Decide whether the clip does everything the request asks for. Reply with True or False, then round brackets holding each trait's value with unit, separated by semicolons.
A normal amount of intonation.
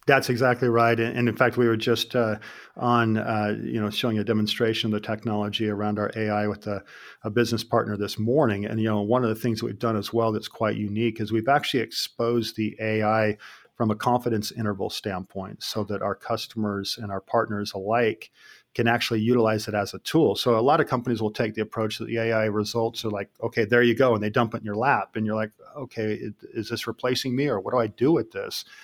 False (1.8 semitones)